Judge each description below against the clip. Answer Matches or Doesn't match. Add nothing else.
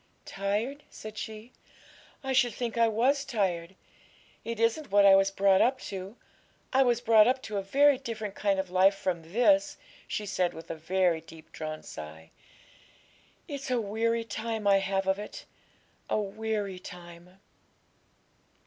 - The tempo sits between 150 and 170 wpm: Matches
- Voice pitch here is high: Matches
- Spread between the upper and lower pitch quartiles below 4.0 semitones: Matches